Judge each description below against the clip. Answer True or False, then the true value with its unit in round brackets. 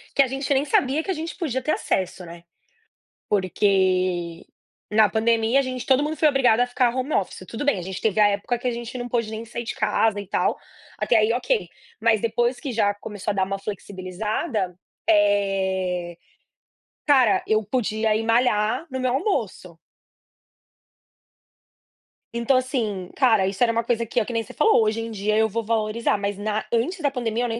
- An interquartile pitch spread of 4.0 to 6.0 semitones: False (3.5 semitones)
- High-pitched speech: True (225 Hz)